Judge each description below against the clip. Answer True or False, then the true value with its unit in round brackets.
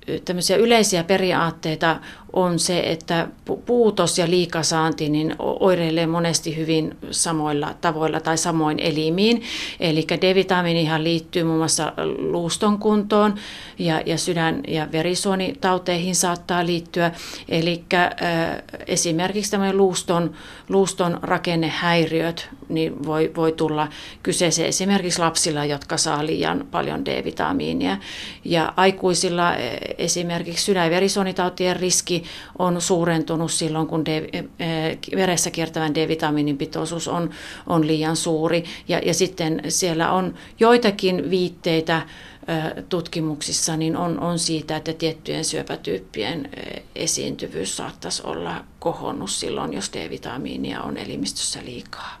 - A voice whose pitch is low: False (170 Hz)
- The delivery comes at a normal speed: True (105 wpm)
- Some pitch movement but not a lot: False (2.1 semitones)